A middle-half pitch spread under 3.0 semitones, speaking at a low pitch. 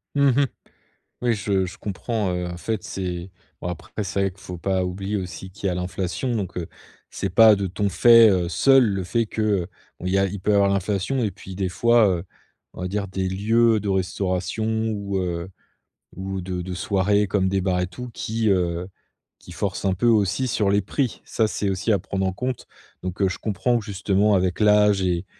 Yes: narrow, 2.5 semitones; very low, 95 Hz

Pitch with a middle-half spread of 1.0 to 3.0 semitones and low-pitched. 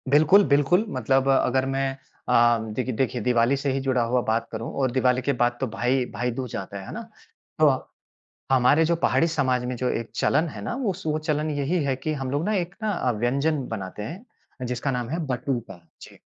No: average, 3.6 semitones; low, 130 Hz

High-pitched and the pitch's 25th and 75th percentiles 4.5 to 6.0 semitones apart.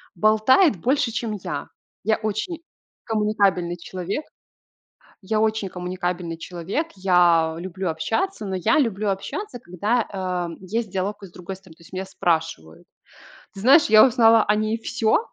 No: high, 195 Hz; average, 3.8 semitones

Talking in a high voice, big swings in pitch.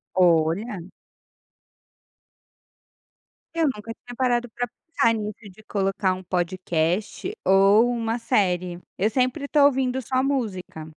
No: high, 215 Hz; average, 5.0 semitones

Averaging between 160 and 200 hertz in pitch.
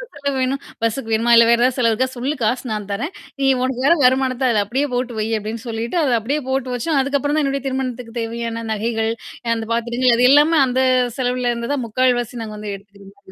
No: high, 245 Hz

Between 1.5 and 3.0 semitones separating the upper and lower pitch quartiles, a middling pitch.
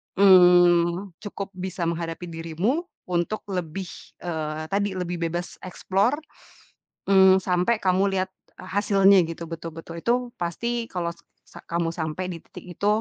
Yes: narrow, 2.5 semitones; medium, 180 Hz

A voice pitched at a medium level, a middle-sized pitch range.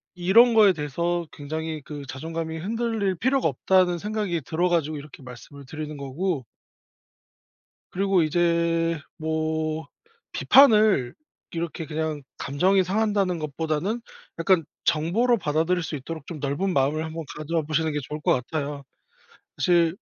Yes: medium, 165 Hz; average, 3.4 semitones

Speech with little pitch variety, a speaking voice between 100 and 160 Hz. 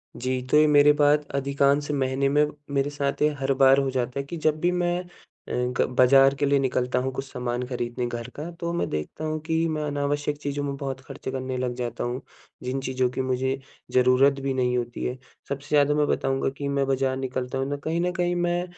Yes: narrow, 2.3 semitones; low, 135 Hz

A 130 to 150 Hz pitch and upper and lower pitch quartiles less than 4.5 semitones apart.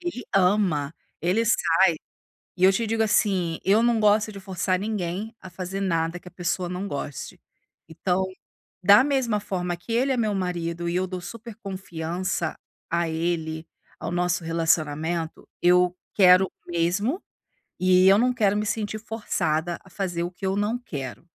No: medium, 185 Hz; average, 3.5 semitones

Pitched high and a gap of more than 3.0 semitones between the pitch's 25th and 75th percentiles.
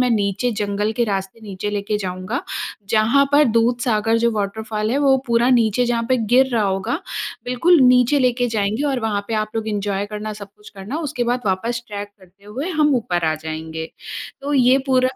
Yes: high, 220 Hz; average, 3.5 semitones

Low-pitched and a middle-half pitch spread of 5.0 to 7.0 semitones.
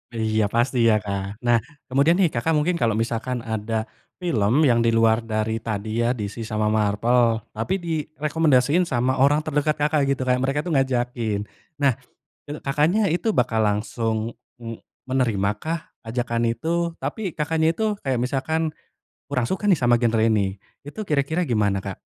Yes: low, 125 Hz; average, 5.3 semitones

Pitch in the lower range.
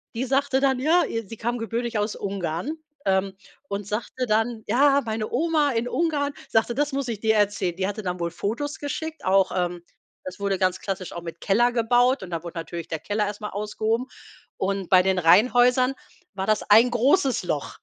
No: high, 220 Hz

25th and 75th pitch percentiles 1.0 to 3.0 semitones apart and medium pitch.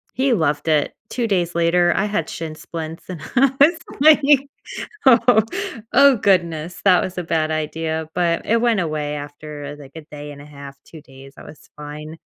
No: average, 4.5 semitones; medium, 165 Hz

